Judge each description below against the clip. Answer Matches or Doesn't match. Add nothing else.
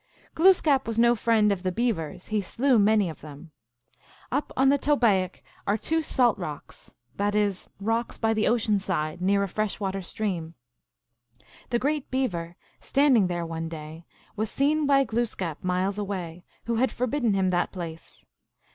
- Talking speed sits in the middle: Matches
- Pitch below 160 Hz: Doesn't match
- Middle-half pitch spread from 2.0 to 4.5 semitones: Doesn't match